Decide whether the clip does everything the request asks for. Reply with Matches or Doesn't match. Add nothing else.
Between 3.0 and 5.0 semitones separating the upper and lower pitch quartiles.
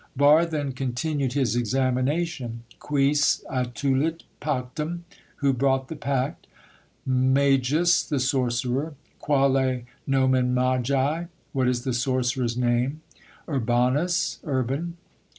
Doesn't match